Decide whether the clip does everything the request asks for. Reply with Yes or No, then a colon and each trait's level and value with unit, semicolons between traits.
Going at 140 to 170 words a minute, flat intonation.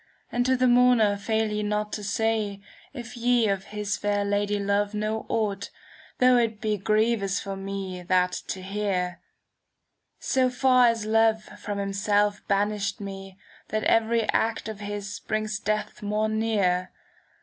Yes: average, 155 wpm; narrow, 1.9 semitones